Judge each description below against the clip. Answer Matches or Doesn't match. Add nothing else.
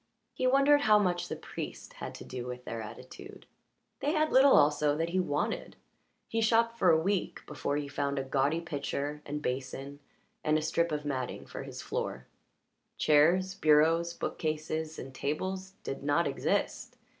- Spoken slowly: Doesn't match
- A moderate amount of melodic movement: Matches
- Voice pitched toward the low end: Doesn't match